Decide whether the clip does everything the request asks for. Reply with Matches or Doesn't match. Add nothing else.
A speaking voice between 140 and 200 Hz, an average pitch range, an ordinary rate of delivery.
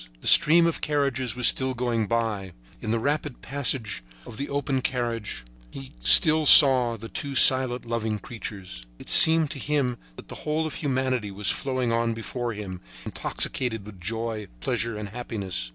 Doesn't match